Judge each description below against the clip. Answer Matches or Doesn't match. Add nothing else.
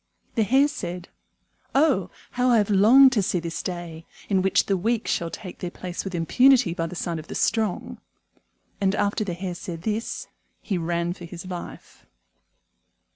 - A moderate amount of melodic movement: Matches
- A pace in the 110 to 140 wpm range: Doesn't match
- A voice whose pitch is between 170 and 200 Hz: Matches